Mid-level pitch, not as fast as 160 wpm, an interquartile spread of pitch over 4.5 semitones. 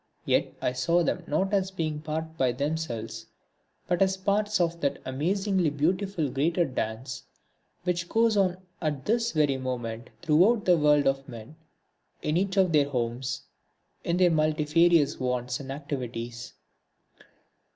Yes: medium, 155 Hz; average, 140 wpm; wide, 5.4 semitones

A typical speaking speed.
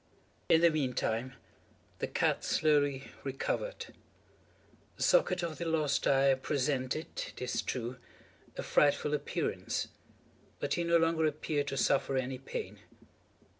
No: slow, 130 wpm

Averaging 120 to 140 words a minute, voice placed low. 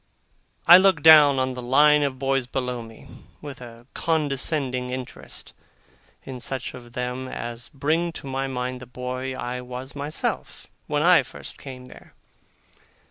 No: average, 150 wpm; low, 130 Hz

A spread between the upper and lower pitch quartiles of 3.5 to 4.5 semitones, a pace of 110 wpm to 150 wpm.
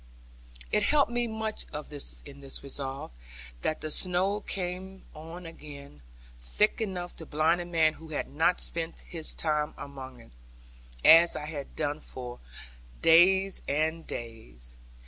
Yes: average, 4.2 semitones; average, 145 wpm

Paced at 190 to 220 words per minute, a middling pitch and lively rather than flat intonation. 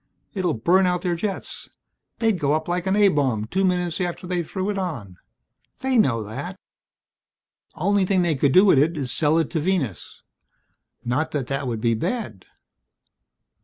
No: average, 175 wpm; medium, 170 Hz; wide, 5.8 semitones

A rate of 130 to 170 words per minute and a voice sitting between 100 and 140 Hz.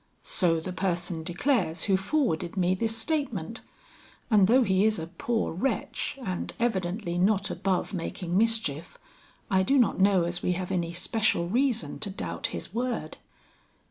No: average, 155 wpm; high, 190 Hz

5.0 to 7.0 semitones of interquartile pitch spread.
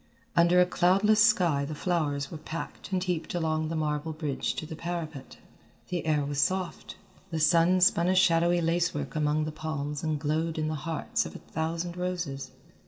No: narrow, 2.4 semitones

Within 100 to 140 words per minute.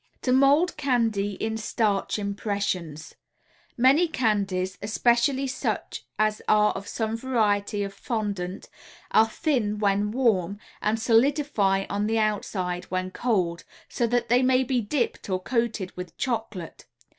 Yes: slow, 135 wpm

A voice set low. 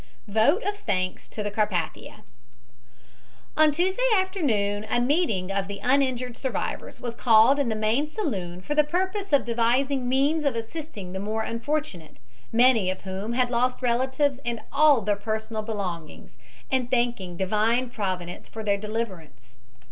No: high, 230 Hz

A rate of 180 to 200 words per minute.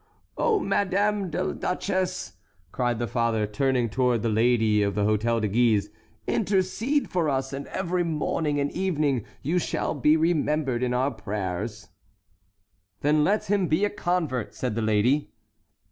No: average, 150 wpm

